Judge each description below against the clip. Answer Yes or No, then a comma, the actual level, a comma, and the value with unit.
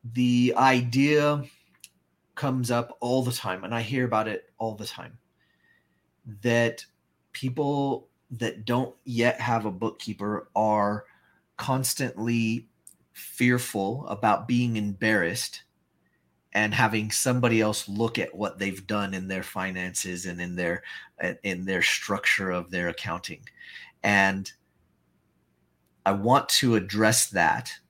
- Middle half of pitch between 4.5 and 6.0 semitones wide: Yes, average, 4.8 semitones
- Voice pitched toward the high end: No, low, 110 Hz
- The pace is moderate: No, slow, 120 wpm